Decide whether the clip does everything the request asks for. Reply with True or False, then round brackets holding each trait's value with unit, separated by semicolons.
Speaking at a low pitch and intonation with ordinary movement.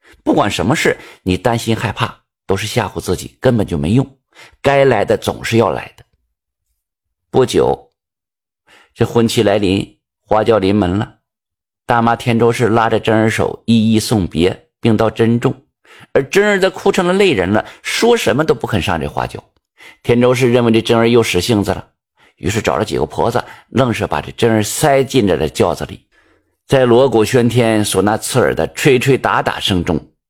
True (115 Hz; 3.5 semitones)